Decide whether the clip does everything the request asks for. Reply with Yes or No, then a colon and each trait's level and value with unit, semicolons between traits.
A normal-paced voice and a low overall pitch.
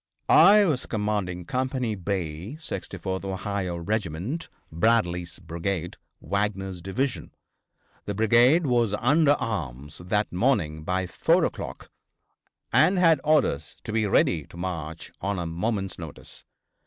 No: slow, 120 wpm; low, 100 Hz